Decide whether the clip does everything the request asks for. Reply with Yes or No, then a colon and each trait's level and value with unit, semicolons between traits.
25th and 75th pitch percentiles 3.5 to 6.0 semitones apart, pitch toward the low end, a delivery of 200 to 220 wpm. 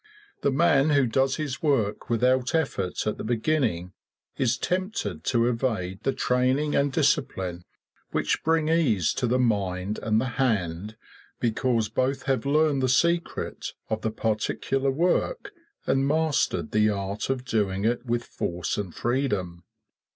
No: average, 4.7 semitones; low, 125 Hz; average, 145 wpm